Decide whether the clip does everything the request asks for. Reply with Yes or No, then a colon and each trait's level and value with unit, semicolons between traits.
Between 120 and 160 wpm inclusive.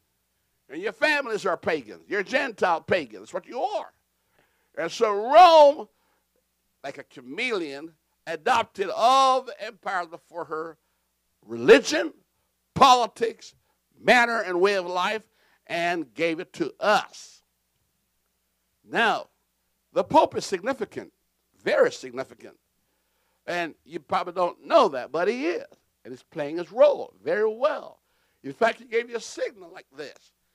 Yes: slow, 135 wpm